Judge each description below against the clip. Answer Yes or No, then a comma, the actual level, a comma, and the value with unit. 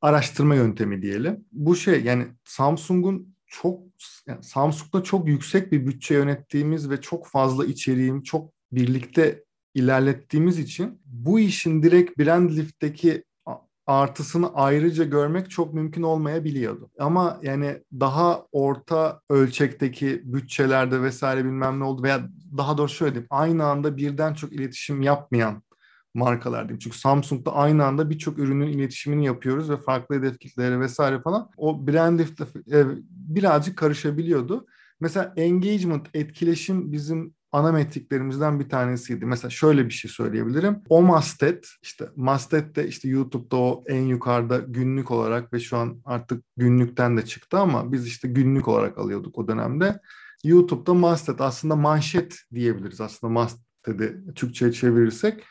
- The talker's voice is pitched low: No, medium, 145 Hz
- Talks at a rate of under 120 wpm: No, average, 135 wpm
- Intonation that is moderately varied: Yes, average, 3.9 semitones